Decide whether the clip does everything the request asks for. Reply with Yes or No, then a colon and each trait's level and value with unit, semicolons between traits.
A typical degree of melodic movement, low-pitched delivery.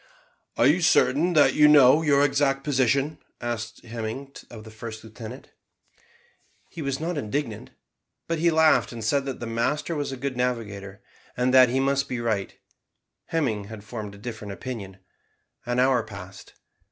Yes: average, 4.2 semitones; low, 125 Hz